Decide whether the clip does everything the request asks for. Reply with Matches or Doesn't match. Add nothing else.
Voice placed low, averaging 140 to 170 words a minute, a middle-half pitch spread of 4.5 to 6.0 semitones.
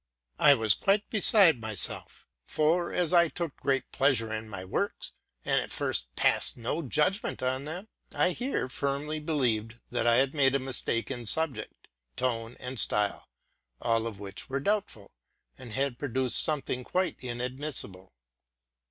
Matches